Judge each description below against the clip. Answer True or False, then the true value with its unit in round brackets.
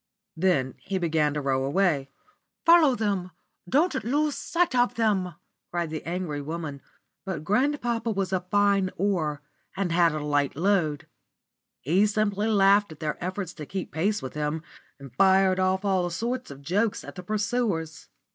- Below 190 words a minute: True (160 wpm)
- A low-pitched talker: False (185 Hz)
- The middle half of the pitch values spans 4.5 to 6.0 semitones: True (4.8 semitones)